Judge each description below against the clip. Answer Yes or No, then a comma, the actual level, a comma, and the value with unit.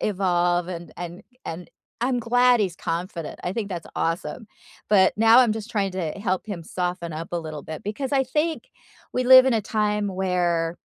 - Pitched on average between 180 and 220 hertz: Yes, high, 190 Hz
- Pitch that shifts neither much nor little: Yes, average, 4.6 semitones